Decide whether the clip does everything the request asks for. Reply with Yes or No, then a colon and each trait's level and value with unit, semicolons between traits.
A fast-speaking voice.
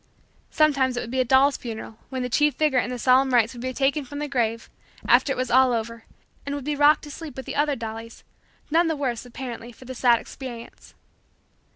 Yes: fast, 225 wpm